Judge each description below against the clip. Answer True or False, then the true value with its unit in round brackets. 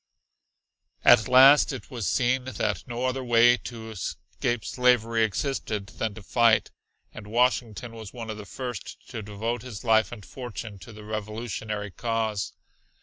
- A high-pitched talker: False (115 Hz)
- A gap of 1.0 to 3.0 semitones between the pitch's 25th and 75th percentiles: True (2.4 semitones)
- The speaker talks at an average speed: True (150 wpm)